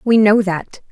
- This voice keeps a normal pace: Yes, average, 195 wpm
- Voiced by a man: No, female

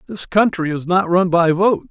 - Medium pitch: Yes, medium, 180 Hz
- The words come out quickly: Yes, fast, 220 wpm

